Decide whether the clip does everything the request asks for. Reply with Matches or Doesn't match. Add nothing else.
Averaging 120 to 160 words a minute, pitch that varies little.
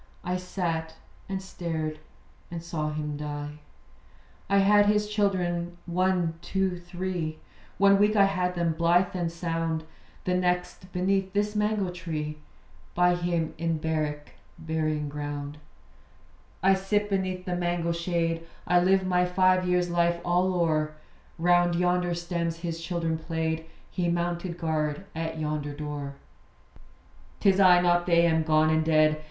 Matches